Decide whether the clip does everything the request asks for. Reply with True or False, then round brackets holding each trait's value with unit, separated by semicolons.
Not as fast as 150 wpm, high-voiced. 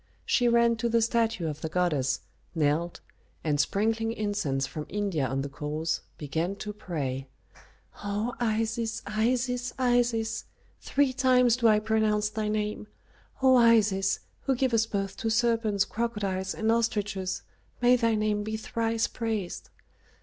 True (140 wpm; 215 Hz)